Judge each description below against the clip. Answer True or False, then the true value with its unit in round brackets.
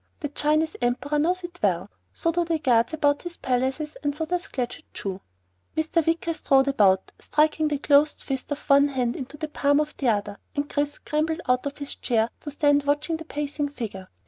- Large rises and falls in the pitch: False (2.9 semitones)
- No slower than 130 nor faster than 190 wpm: False (200 wpm)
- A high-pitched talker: True (290 Hz)